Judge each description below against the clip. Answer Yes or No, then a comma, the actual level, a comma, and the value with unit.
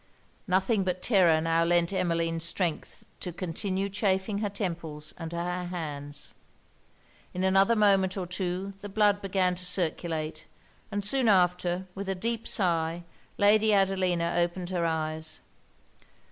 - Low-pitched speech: No, medium, 180 Hz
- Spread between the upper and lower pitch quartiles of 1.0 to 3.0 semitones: Yes, average, 2.7 semitones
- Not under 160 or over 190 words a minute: No, slow, 135 wpm